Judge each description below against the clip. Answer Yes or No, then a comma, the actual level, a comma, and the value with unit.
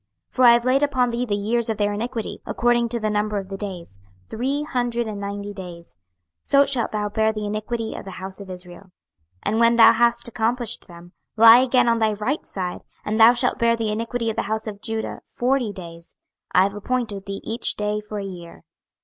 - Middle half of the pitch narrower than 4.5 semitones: Yes, average, 2.8 semitones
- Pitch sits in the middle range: No, high, 220 Hz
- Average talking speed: No, fast, 220 wpm